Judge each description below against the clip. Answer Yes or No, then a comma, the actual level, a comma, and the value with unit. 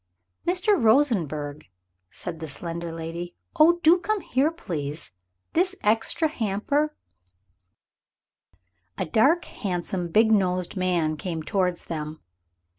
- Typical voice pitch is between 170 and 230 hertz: Yes, medium, 185 Hz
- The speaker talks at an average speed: No, slow, 115 wpm